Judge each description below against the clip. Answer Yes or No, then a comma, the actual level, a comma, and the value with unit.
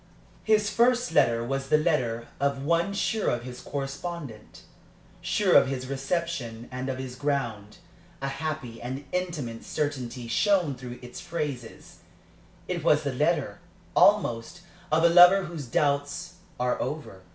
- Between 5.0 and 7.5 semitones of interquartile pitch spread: Yes, wide, 5.4 semitones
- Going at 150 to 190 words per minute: No, average, 140 wpm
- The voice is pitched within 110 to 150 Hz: Yes, medium, 140 Hz